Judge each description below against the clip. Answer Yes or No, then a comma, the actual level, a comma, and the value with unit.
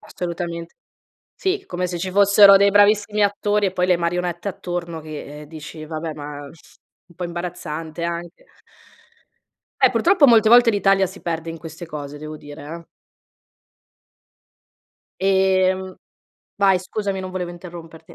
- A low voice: No, medium, 175 Hz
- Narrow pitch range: No, average, 3.1 semitones